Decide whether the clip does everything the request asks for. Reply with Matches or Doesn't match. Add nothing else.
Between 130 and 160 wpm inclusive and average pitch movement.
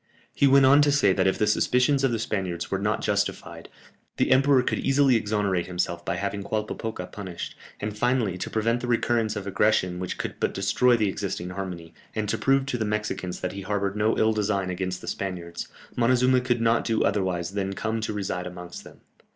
Doesn't match